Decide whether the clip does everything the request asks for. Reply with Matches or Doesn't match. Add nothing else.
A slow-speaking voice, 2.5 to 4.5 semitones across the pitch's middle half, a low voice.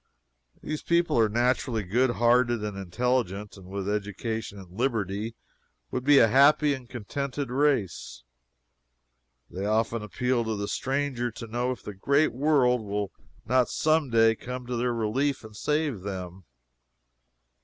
Doesn't match